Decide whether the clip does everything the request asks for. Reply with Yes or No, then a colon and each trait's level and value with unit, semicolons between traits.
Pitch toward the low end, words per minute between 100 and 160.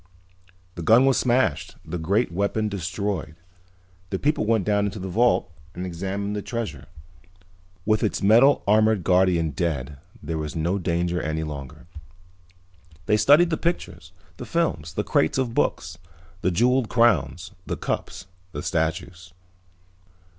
Yes: very low, 95 Hz; average, 140 wpm